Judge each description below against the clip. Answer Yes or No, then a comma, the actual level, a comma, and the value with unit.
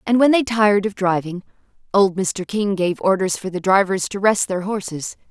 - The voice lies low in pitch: No, high, 195 Hz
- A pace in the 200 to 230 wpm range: Yes, fast, 205 wpm